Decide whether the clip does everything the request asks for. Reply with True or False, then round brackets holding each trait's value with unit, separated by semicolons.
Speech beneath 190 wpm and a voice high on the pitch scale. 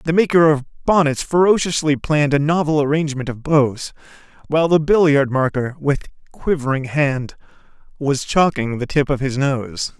False (150 wpm; 145 Hz)